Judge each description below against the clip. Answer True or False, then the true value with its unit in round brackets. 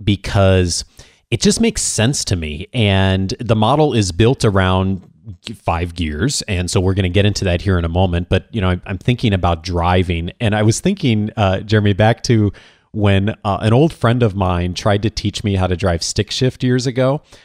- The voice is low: True (100 Hz)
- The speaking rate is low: False (205 wpm)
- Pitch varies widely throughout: False (3.6 semitones)